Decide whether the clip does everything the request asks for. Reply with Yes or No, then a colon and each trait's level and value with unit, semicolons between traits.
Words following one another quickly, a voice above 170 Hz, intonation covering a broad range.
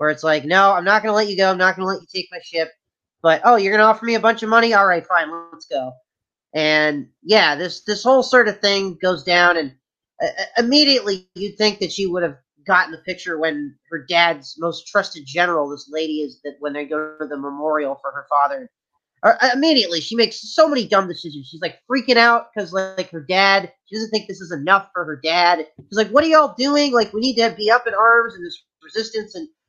Yes: fast, 245 wpm; medium, 185 Hz; wide, 5.8 semitones